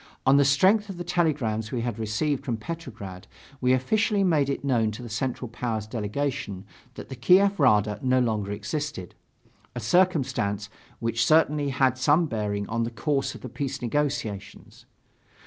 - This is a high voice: No, low, 130 Hz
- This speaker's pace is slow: No, average, 165 wpm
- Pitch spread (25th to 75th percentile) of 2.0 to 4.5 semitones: No, average, 5.2 semitones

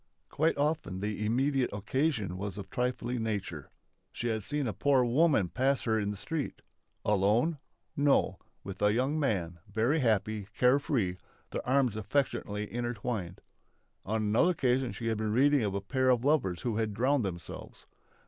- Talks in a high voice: No, low, 115 Hz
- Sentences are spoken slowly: No, average, 165 wpm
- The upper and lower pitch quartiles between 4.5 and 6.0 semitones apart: Yes, average, 4.8 semitones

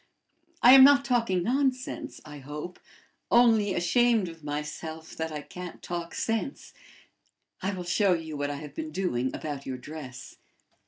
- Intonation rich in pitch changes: Yes, wide, 7.0 semitones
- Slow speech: No, average, 155 wpm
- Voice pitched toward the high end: No, medium, 170 Hz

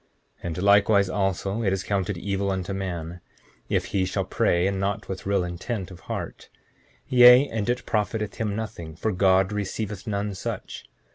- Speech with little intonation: Yes, narrow, 2.1 semitones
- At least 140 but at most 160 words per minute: No, average, 180 wpm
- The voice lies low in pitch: Yes, low, 100 Hz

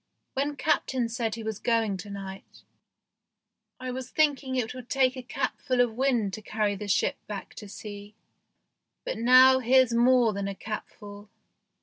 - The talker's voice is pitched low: No, high, 230 Hz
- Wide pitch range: No, average, 3.7 semitones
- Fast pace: No, average, 170 wpm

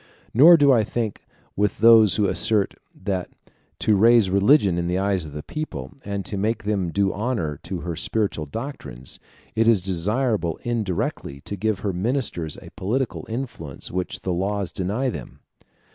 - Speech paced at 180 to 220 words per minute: No, average, 165 wpm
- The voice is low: Yes, low, 100 Hz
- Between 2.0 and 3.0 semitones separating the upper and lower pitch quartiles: No, average, 4.1 semitones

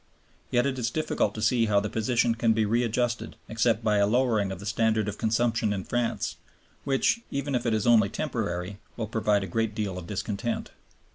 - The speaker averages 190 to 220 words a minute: Yes, average, 200 wpm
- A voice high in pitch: No, low, 110 Hz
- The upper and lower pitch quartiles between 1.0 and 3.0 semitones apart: Yes, narrow, 2.6 semitones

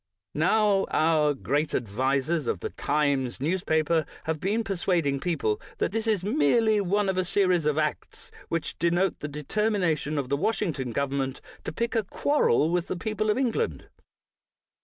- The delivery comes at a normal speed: Yes, average, 160 wpm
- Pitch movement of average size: No, wide, 5.9 semitones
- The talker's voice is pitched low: No, medium, 165 Hz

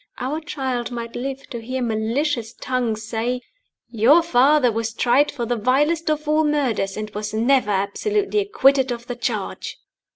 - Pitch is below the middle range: No, very high, 250 Hz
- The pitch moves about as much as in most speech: Yes, average, 4.3 semitones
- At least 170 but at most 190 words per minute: No, average, 160 wpm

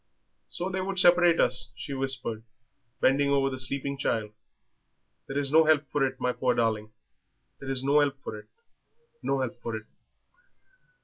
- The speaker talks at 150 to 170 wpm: Yes, average, 165 wpm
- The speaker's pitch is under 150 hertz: Yes, low, 135 Hz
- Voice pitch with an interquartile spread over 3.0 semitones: No, narrow, 2.6 semitones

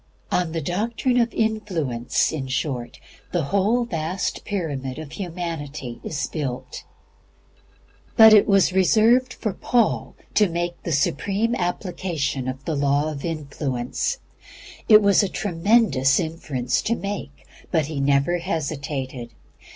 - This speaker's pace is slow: Yes, slow, 130 wpm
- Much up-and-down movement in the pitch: Yes, wide, 6.2 semitones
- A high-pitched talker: No, medium, 165 Hz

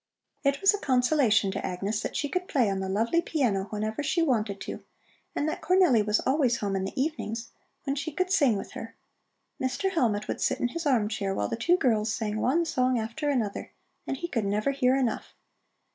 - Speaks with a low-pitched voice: No, high, 245 Hz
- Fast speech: Yes, fast, 210 wpm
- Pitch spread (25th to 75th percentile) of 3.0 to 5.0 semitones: No, wide, 5.6 semitones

